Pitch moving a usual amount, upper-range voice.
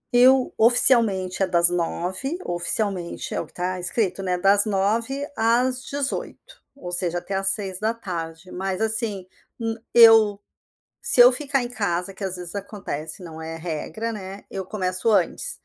Yes: average, 4.2 semitones; high, 195 Hz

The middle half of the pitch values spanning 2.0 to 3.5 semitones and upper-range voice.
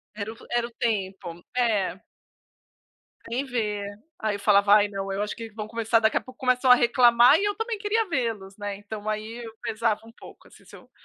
Yes: average, 2.9 semitones; high, 225 Hz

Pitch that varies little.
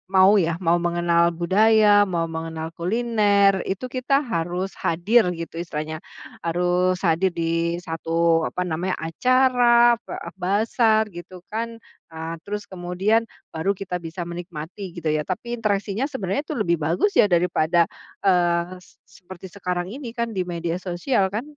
No: average, 3.6 semitones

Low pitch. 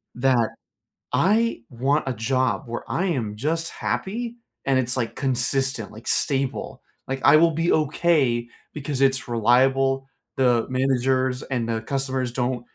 Yes: low, 130 Hz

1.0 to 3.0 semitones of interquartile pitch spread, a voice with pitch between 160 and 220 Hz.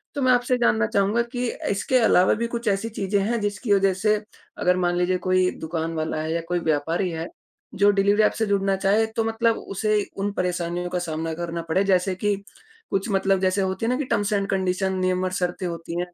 Yes: narrow, 2.6 semitones; high, 190 Hz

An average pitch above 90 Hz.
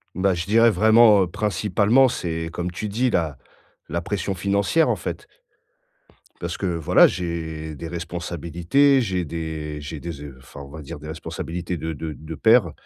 No: very low, 85 Hz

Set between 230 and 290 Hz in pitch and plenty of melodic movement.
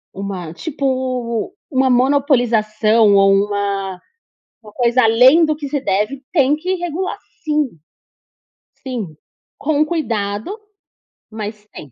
Yes: high, 245 Hz; wide, 5.7 semitones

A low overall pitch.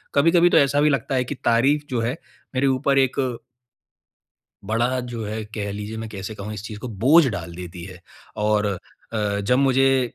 Yes: low, 120 Hz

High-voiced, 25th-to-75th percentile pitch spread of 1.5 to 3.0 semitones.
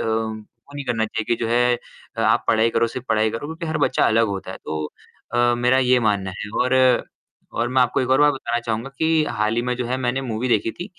No: low, 120 Hz; average, 2.7 semitones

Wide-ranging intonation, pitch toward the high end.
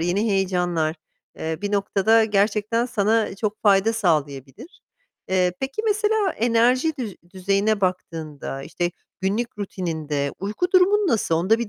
No: average, 4.5 semitones; high, 200 Hz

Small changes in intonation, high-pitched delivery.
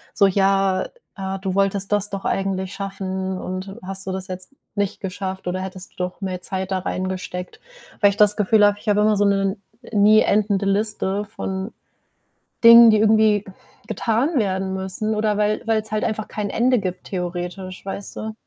Yes: narrow, 1.8 semitones; high, 195 Hz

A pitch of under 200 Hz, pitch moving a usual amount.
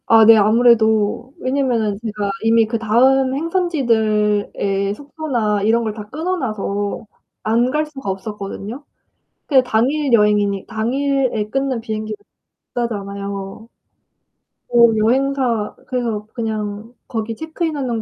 No: high, 225 Hz; average, 3.9 semitones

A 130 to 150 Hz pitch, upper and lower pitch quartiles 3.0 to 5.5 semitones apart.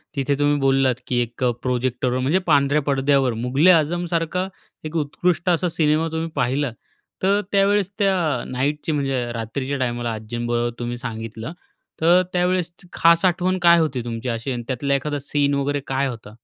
Yes: medium, 140 Hz; average, 4.9 semitones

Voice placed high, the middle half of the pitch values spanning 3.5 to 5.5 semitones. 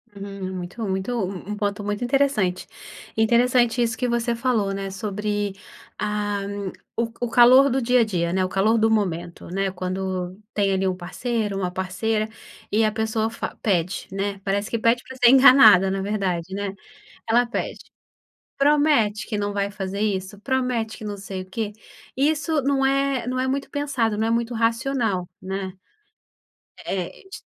Yes: high, 210 Hz; average, 3.8 semitones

